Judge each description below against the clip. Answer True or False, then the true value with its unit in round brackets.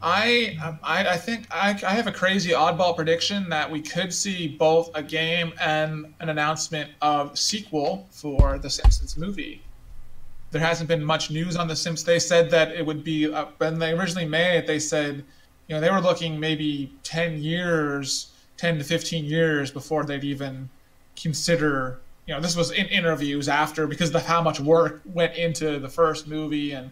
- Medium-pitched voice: True (160 Hz)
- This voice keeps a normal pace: True (185 wpm)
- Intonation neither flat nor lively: False (2.2 semitones)